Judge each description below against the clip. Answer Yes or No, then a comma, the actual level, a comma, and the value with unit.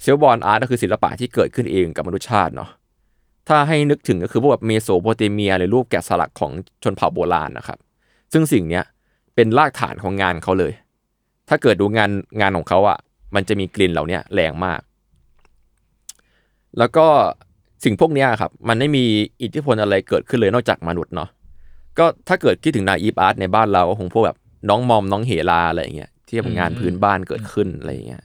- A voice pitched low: Yes, low, 100 Hz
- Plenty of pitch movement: No, average, 4.3 semitones